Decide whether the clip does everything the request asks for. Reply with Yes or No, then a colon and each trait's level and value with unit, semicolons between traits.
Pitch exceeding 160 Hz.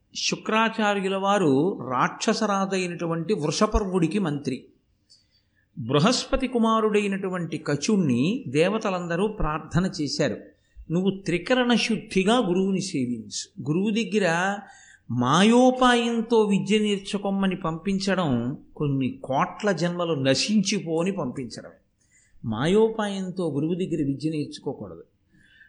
Yes: medium, 185 Hz